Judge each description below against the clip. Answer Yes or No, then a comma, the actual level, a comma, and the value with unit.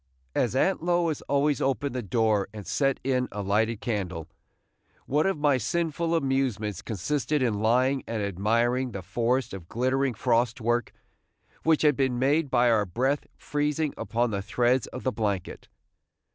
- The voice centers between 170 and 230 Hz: No, low, 125 Hz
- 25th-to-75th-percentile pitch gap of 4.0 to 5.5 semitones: Yes, average, 4.4 semitones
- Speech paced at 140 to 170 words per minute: Yes, average, 160 wpm